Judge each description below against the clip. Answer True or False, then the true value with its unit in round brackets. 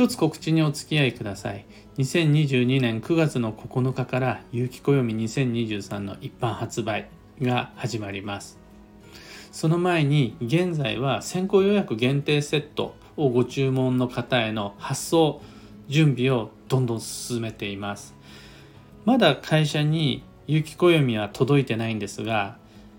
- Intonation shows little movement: False (5.3 semitones)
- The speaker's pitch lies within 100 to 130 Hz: True (125 Hz)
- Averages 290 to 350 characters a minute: False (255 characters per minute)